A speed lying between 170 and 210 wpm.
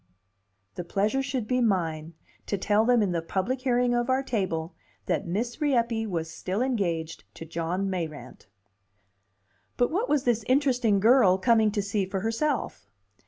No: average, 160 wpm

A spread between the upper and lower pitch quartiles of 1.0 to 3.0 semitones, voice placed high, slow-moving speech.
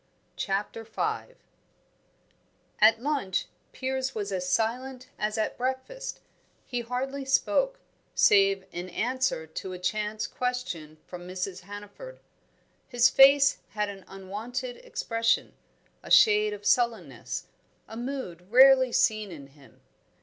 No: average, 5.3 semitones; high, 225 Hz; slow, 120 wpm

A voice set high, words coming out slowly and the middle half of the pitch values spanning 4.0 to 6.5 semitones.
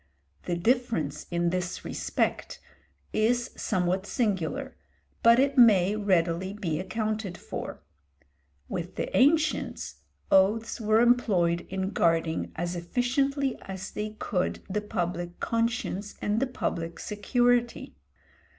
Yes: high, 205 Hz; slow, 115 wpm; average, 5.2 semitones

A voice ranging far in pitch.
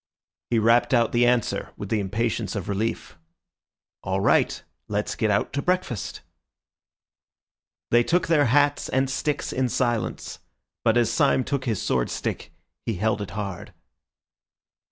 No: average, 4.0 semitones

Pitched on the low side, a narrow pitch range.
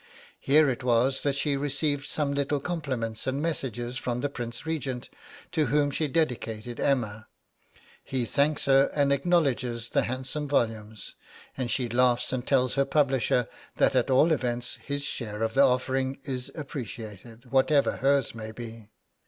No: low, 130 Hz; average, 3.0 semitones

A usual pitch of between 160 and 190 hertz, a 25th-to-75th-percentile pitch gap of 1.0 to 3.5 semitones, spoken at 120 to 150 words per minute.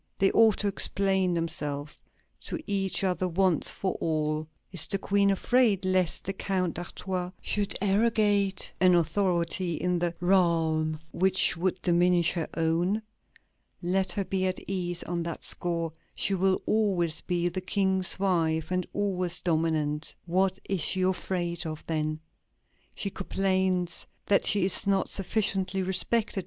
Yes: medium, 185 Hz; narrow, 2.4 semitones; average, 145 wpm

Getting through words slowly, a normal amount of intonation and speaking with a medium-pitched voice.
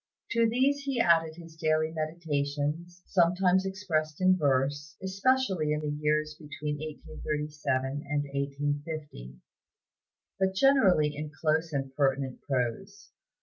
Yes: slow, 115 wpm; average, 3.8 semitones; medium, 155 Hz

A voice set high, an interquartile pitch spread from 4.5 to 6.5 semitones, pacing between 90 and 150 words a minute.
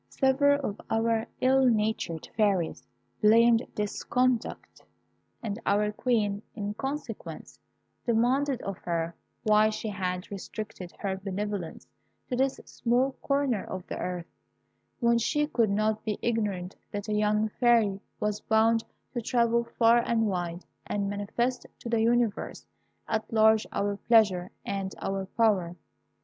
No: high, 215 Hz; average, 2.9 semitones; slow, 135 wpm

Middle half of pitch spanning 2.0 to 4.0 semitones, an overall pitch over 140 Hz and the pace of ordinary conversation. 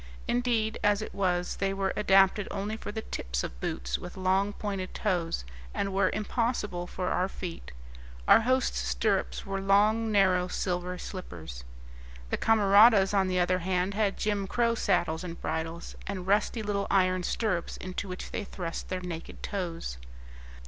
Yes: narrow, 2.6 semitones; high, 190 Hz; average, 160 wpm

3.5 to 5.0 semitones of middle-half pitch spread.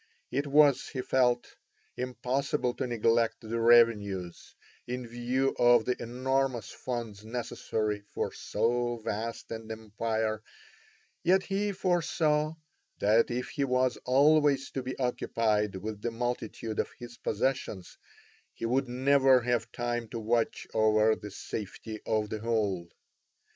No: average, 2.8 semitones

